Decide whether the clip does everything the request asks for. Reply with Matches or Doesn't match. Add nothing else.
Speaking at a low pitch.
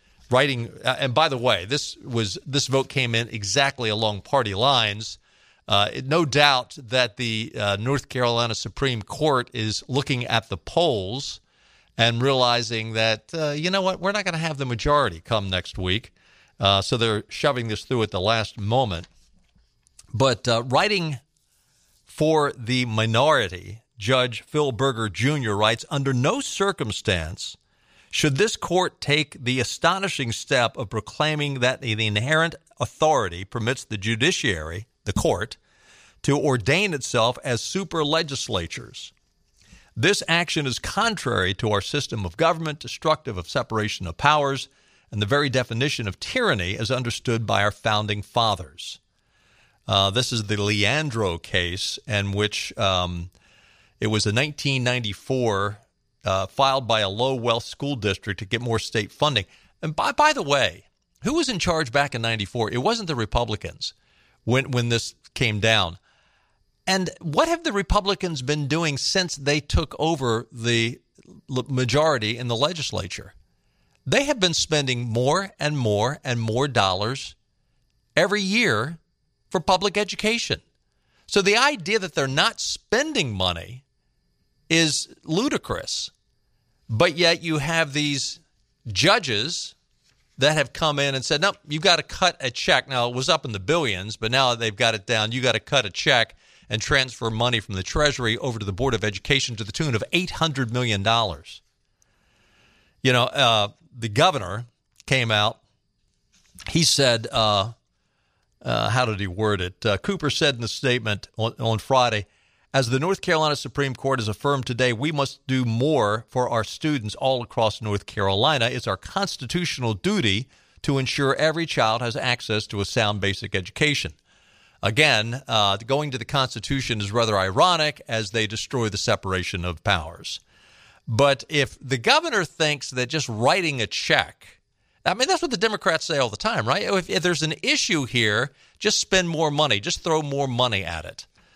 Matches